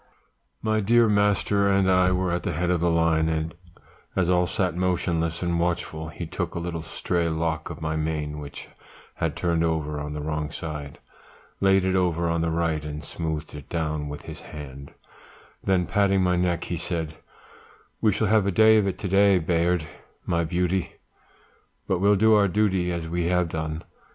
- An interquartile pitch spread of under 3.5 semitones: Yes, average, 2.9 semitones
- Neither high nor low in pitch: No, very low, 85 Hz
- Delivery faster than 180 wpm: Yes, average, 190 wpm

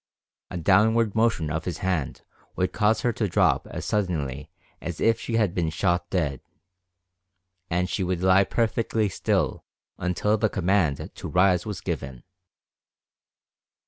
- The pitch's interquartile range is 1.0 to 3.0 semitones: No, average, 3.7 semitones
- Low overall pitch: Yes, very low, 95 Hz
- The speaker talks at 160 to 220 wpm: No, average, 145 wpm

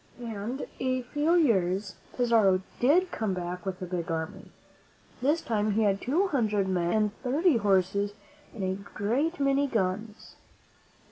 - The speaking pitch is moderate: No, high, 215 Hz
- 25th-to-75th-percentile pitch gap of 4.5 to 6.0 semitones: Yes, wide, 5.4 semitones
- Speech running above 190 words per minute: No, average, 150 wpm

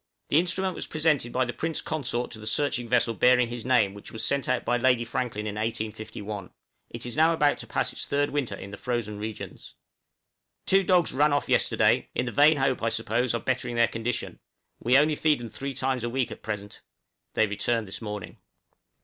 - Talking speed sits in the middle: No, fast, 215 wpm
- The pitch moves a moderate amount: Yes, average, 4.0 semitones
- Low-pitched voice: Yes, low, 120 Hz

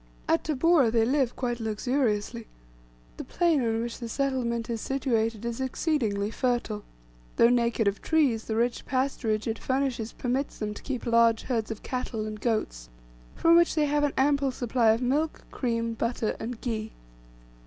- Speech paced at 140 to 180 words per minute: Yes, average, 165 wpm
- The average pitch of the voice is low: No, high, 235 Hz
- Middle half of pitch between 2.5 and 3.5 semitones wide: Yes, average, 3.1 semitones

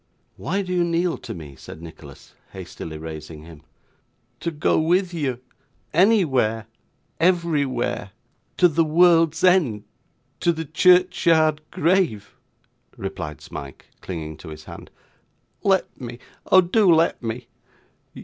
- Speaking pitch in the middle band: Yes, medium, 155 Hz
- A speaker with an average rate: No, slow, 120 wpm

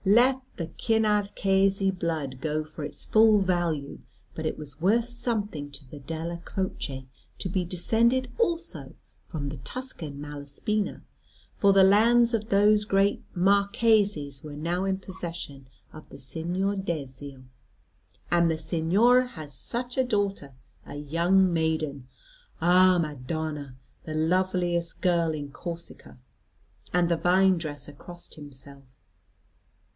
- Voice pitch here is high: No, medium, 175 Hz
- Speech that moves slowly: Yes, slow, 130 wpm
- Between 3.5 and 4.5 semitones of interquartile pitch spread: No, average, 5.1 semitones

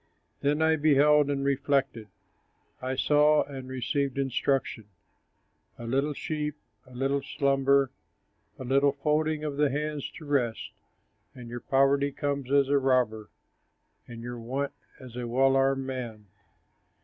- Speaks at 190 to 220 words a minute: No, slow, 135 wpm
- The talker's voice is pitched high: No, low, 135 Hz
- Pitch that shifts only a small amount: Yes, narrow, 1.9 semitones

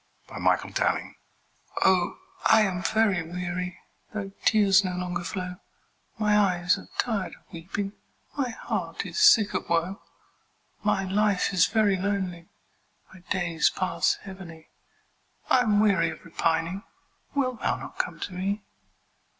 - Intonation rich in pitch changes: No, average, 2.7 semitones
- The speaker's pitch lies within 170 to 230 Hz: Yes, high, 190 Hz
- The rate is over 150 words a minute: No, slow, 135 wpm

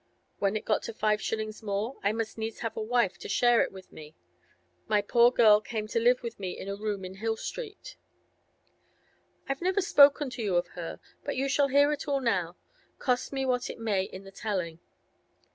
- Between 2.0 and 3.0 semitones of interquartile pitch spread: No, average, 4.2 semitones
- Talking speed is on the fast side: Yes, fast, 210 wpm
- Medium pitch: No, high, 225 Hz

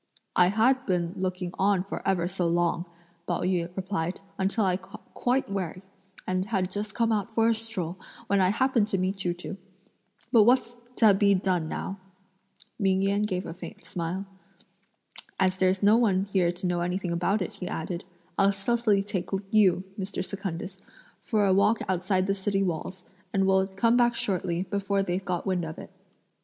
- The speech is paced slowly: No, average, 180 wpm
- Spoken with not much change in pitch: Yes, narrow, 2.0 semitones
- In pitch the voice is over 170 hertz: Yes, high, 190 Hz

